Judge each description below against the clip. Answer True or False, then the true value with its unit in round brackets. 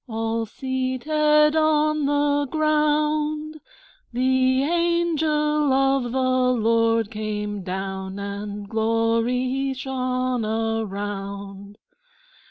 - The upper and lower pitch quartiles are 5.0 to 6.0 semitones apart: True (5.3 semitones)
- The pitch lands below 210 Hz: False (255 Hz)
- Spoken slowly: True (75 wpm)